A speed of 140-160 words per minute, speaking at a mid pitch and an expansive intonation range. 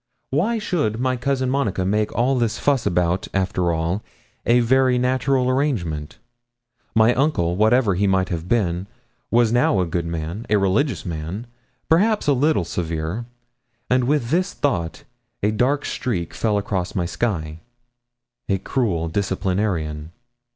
No: average, 145 wpm; low, 105 Hz; wide, 6.6 semitones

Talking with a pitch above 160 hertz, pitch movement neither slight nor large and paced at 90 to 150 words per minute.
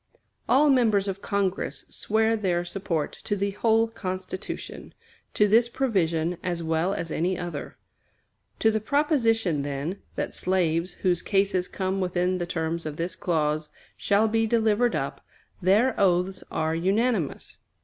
Yes: high, 190 Hz; average, 4.2 semitones; average, 140 wpm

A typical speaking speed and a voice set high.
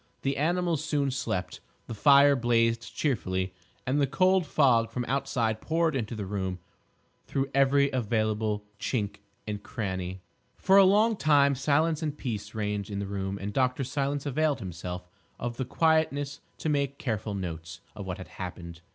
No: average, 160 wpm; low, 125 Hz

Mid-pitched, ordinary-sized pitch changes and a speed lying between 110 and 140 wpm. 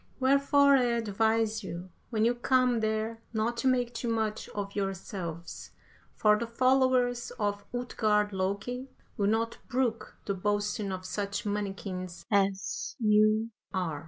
No: high, 215 Hz; average, 3.1 semitones; slow, 135 wpm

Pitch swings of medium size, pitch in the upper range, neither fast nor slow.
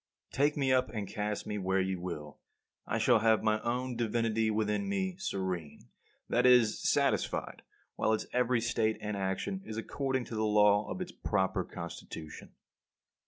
No: average, 3.4 semitones; low, 110 Hz; average, 165 wpm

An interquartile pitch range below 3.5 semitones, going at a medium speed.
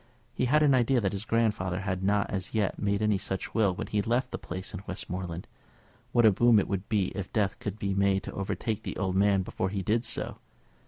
No: narrow, 2.5 semitones; fast, 230 wpm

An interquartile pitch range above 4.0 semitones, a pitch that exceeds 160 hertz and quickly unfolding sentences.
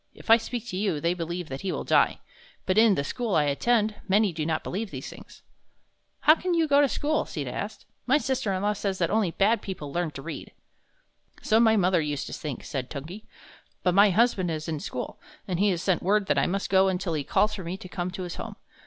Yes: average, 4.4 semitones; high, 190 Hz; fast, 240 wpm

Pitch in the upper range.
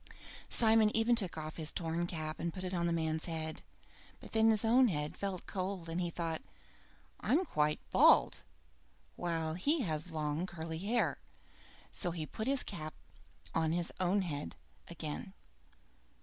No: medium, 170 Hz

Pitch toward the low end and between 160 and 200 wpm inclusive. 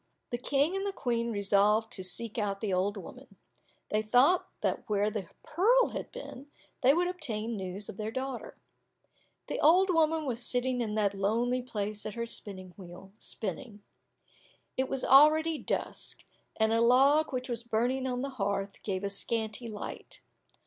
No: high, 235 Hz; average, 170 wpm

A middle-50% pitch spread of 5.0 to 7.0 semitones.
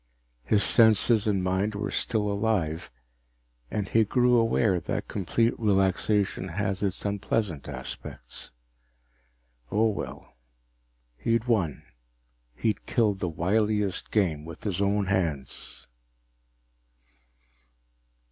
No: average, 2.9 semitones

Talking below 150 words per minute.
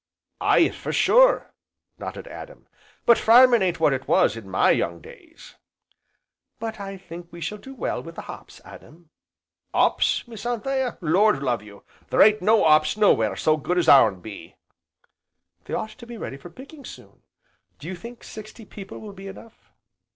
No: average, 175 wpm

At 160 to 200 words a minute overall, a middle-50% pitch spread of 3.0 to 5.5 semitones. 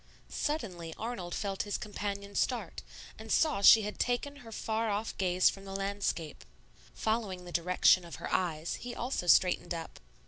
Yes: average, 165 wpm; average, 3.7 semitones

